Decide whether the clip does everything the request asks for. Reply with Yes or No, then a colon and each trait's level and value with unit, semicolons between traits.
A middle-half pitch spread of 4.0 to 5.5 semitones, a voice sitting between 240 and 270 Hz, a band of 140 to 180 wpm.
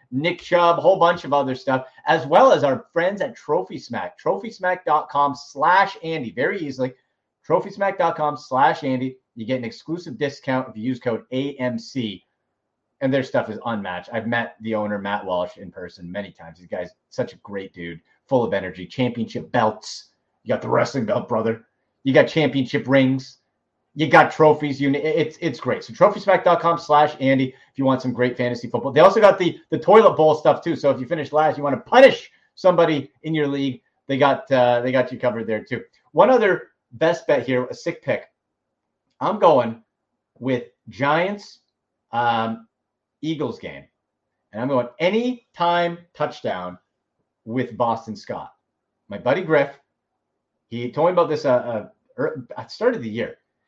No: average, 5.1 semitones; low, 135 Hz; average, 175 wpm